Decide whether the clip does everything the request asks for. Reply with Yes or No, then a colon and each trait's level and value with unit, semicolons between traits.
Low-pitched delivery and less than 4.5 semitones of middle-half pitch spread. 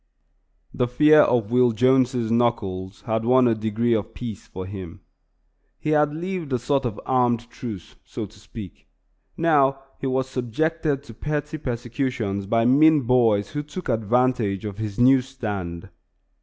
Yes: low, 120 Hz; average, 3.7 semitones